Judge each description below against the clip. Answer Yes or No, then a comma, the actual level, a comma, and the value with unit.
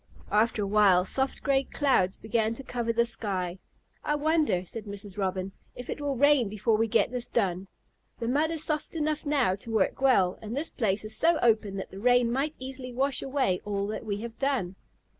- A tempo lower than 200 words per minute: No, fast, 205 wpm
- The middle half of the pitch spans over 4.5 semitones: Yes, average, 5.2 semitones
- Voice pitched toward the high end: Yes, high, 230 Hz